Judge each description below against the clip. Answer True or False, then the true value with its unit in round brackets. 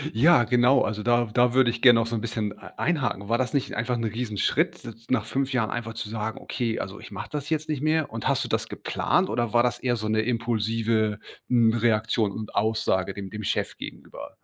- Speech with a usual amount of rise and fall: False (2.2 semitones)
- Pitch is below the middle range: True (115 Hz)